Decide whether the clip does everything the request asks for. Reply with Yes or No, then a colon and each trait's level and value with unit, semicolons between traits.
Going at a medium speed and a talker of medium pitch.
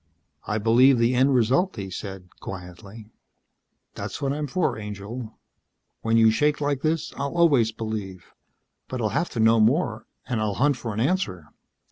No: average, 165 wpm; low, 115 Hz